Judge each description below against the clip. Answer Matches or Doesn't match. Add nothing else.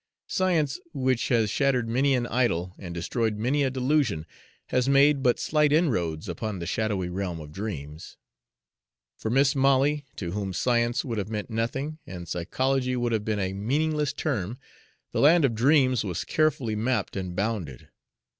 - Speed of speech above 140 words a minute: Matches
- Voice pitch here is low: Matches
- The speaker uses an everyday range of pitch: Doesn't match